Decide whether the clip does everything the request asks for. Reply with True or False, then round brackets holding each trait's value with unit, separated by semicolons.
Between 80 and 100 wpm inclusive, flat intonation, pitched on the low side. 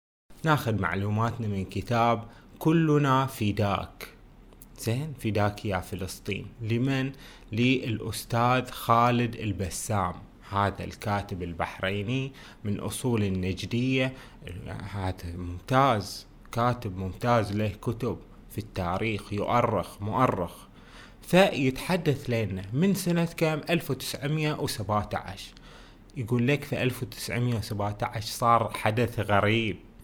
False (90 wpm; 4.2 semitones; 110 Hz)